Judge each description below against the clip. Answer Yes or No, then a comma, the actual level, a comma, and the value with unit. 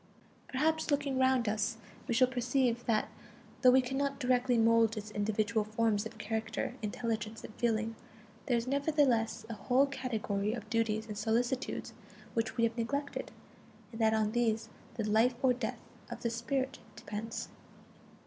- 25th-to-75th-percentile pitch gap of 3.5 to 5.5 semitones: No, average, 2.7 semitones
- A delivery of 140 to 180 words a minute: Yes, average, 155 wpm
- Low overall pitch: No, high, 230 Hz